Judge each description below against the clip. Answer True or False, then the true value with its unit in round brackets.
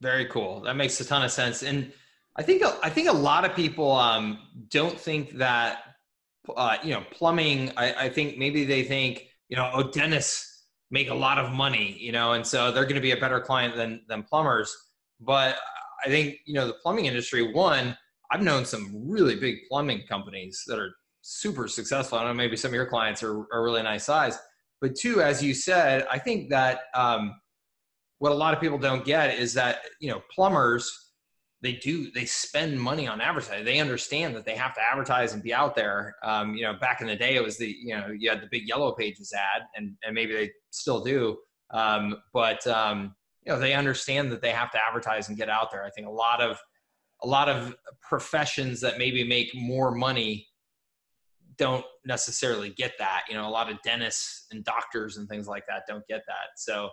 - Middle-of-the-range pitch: False (125 Hz)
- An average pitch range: True (3.9 semitones)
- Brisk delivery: True (210 wpm)